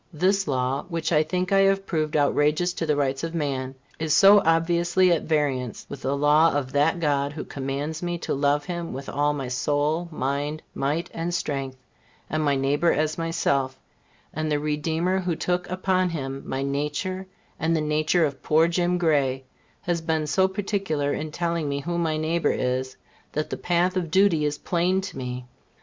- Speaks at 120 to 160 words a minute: No, average, 185 wpm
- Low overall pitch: No, medium, 155 Hz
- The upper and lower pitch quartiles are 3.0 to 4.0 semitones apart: Yes, average, 3.4 semitones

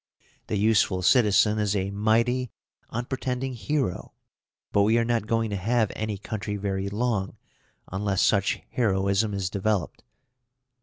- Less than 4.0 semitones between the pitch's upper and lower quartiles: Yes, average, 2.8 semitones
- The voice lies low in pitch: Yes, low, 105 Hz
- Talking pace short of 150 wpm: Yes, slow, 135 wpm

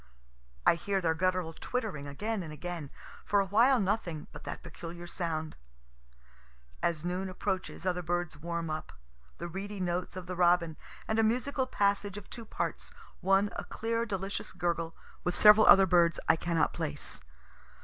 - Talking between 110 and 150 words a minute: No, average, 160 wpm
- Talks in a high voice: No, medium, 180 Hz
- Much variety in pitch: No, average, 3.3 semitones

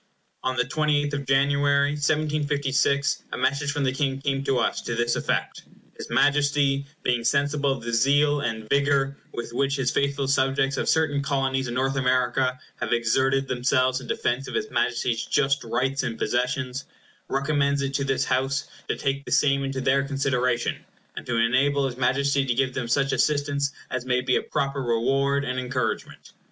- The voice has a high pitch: No, low, 135 Hz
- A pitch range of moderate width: No, narrow, 1.8 semitones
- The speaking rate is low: No, average, 180 wpm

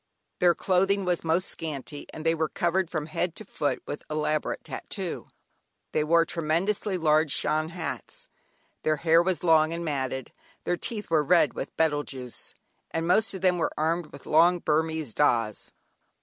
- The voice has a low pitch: No, medium, 160 Hz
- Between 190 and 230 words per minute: No, average, 170 wpm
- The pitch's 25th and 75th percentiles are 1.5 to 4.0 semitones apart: Yes, narrow, 2.6 semitones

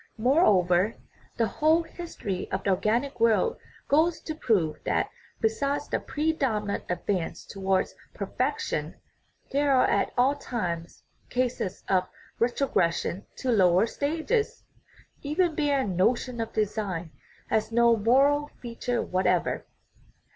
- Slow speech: Yes, slow, 120 wpm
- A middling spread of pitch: No, wide, 6.7 semitones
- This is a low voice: No, high, 230 Hz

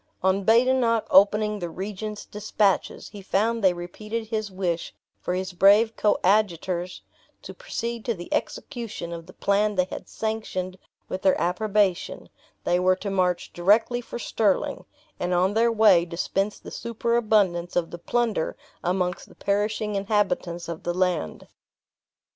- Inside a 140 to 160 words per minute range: Yes, average, 145 wpm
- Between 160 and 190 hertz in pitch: No, high, 200 Hz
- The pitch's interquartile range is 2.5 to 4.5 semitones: Yes, average, 3.3 semitones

